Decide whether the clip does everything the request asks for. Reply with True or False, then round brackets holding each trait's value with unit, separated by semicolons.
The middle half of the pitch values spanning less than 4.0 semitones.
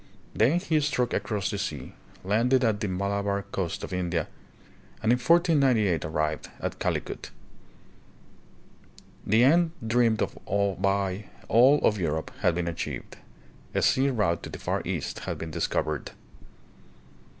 False (5.6 semitones)